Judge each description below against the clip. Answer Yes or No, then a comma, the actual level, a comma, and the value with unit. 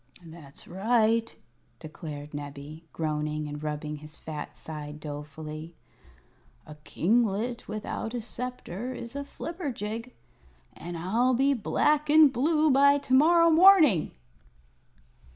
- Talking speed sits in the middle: No, slow, 115 wpm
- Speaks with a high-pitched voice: Yes, high, 215 Hz